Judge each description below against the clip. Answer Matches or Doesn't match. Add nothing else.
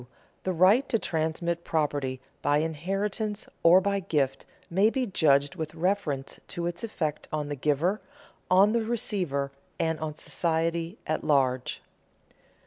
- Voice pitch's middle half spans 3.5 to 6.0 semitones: Matches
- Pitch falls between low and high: Matches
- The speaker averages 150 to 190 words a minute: Doesn't match